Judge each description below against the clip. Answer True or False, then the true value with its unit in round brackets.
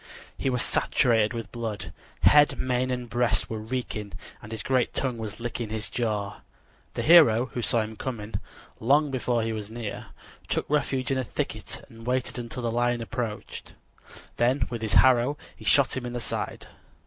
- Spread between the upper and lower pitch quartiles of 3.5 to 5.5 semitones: False (2.4 semitones)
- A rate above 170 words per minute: True (180 wpm)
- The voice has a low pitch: True (120 Hz)